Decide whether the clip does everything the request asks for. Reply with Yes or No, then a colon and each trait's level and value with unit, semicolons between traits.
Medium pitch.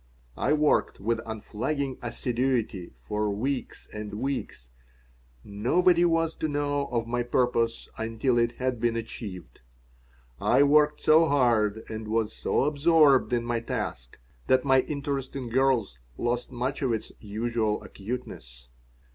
No: low, 120 Hz